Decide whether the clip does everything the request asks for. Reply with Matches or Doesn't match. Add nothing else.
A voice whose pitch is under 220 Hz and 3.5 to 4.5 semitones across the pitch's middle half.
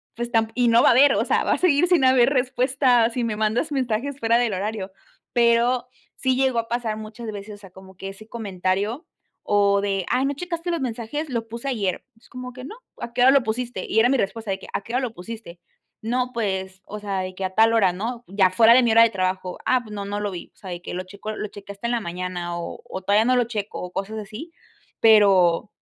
Doesn't match